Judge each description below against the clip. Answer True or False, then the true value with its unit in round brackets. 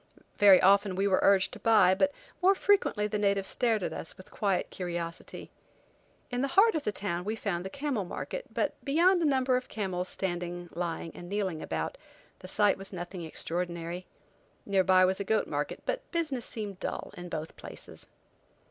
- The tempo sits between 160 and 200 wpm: True (185 wpm)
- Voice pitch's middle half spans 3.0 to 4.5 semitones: False (5.1 semitones)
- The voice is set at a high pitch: True (195 Hz)